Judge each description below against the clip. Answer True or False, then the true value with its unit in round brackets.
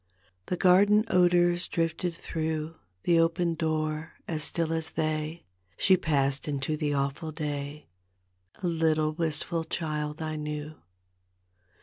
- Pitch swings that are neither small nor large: False (1.8 semitones)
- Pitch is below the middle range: False (160 Hz)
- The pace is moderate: False (120 wpm)